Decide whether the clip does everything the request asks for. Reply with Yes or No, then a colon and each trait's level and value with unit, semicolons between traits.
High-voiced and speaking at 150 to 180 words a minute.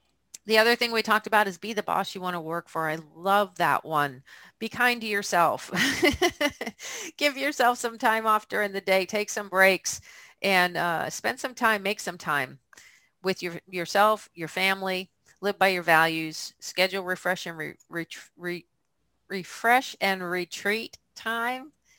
Yes: high, 195 Hz; average, 165 wpm